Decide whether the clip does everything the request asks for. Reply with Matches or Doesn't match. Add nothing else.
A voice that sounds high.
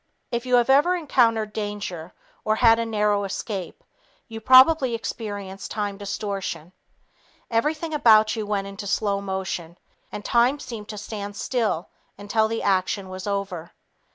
Matches